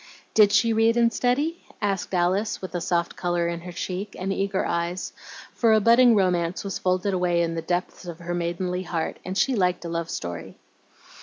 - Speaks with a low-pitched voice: No, medium, 185 Hz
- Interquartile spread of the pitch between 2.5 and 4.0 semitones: Yes, average, 3.1 semitones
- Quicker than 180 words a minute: Yes, average, 200 wpm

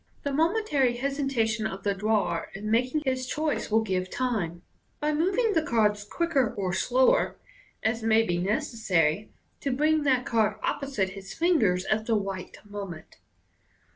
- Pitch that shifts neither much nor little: No, wide, 5.8 semitones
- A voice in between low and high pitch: No, high, 225 Hz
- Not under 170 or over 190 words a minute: No, average, 155 wpm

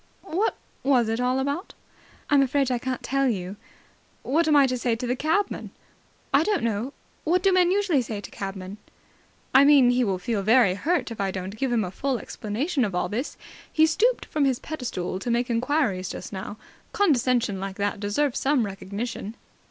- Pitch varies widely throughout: Yes, wide, 5.8 semitones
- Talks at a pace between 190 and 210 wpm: Yes, average, 195 wpm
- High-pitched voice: Yes, very high, 250 Hz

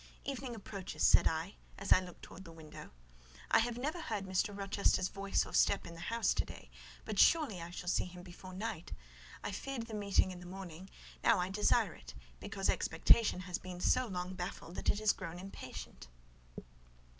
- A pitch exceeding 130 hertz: Yes, high, 190 Hz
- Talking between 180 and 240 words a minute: Yes, average, 190 wpm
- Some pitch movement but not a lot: Yes, average, 3.2 semitones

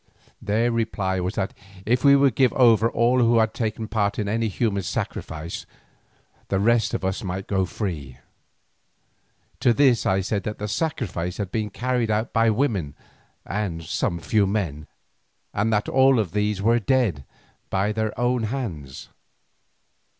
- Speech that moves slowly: No, average, 155 wpm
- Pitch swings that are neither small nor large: Yes, average, 3.5 semitones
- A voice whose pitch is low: Yes, low, 105 Hz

